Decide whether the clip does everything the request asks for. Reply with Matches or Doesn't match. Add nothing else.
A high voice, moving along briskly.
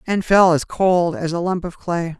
Doesn't match